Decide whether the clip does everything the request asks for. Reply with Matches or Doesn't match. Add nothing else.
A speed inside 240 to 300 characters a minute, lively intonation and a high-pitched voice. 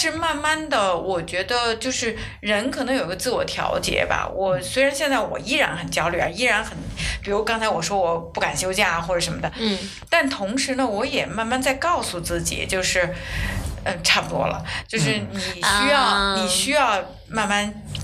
Matches